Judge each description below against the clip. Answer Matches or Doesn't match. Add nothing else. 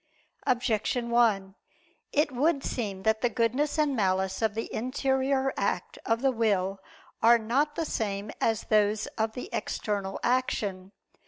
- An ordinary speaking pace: Matches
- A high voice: Matches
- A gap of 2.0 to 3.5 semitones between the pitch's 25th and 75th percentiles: Doesn't match